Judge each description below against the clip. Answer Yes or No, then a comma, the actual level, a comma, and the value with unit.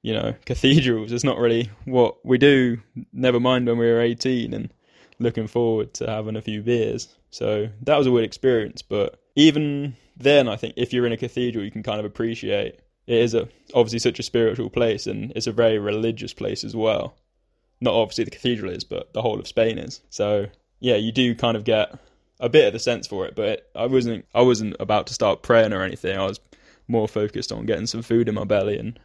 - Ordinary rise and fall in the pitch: No, narrow, 1.9 semitones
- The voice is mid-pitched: No, low, 115 Hz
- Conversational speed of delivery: No, fast, 225 wpm